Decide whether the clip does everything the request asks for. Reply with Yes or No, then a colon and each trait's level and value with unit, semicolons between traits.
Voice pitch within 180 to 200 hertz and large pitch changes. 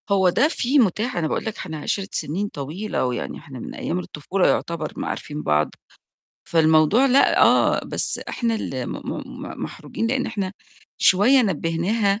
Yes: high, 190 Hz; wide, 6.1 semitones